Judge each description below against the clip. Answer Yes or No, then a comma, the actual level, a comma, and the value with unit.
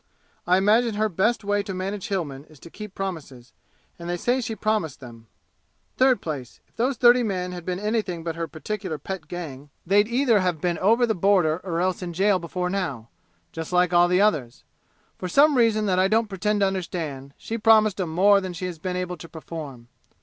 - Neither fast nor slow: No, fast, 210 wpm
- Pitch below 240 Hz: Yes, medium, 185 Hz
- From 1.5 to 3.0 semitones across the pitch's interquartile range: No, average, 4.1 semitones